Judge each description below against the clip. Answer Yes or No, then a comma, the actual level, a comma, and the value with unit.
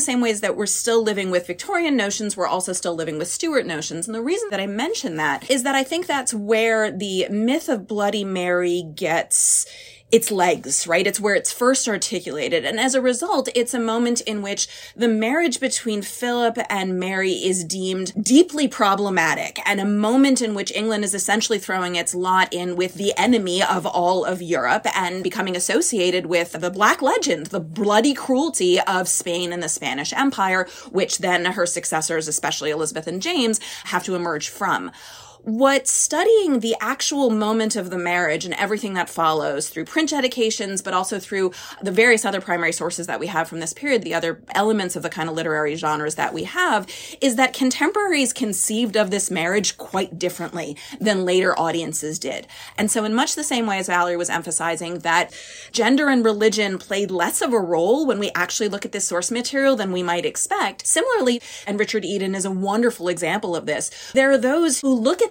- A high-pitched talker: Yes, high, 200 Hz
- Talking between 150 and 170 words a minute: No, average, 195 wpm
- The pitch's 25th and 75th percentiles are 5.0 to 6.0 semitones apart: Yes, average, 5.3 semitones